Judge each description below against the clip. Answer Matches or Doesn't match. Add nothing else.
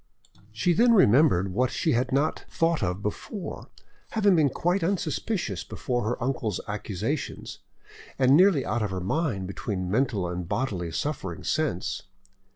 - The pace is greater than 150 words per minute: Doesn't match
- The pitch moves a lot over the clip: Matches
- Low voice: Matches